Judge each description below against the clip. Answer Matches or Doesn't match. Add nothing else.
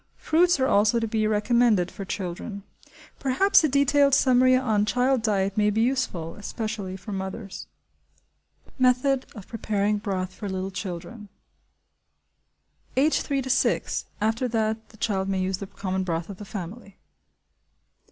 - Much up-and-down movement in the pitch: Doesn't match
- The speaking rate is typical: Matches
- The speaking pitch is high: Matches